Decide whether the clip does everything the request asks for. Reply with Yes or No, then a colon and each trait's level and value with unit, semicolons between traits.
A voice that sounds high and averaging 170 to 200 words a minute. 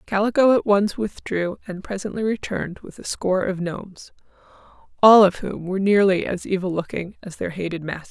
Yes: high, 195 Hz; average, 180 wpm